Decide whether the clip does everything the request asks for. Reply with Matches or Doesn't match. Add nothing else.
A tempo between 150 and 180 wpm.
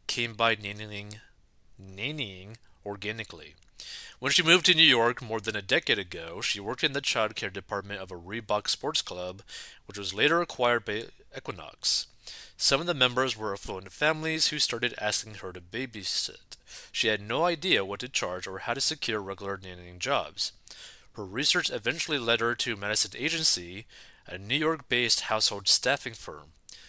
Matches